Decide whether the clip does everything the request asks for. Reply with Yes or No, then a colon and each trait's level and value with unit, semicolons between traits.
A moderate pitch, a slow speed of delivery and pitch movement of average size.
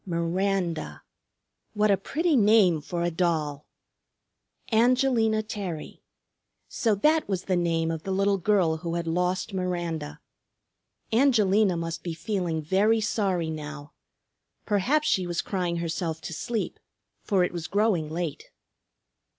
Yes: medium, 180 Hz; slow, 130 wpm; average, 4.0 semitones